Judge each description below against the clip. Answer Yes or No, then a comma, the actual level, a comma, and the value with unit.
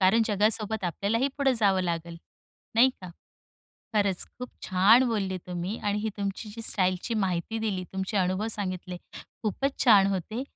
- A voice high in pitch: Yes, high, 200 Hz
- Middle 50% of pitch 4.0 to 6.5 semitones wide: No, average, 3.1 semitones